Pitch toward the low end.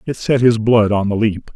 Yes: low, 110 Hz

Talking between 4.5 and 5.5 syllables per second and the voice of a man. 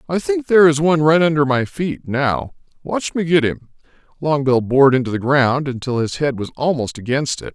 Yes: 5.4 syllables/s; male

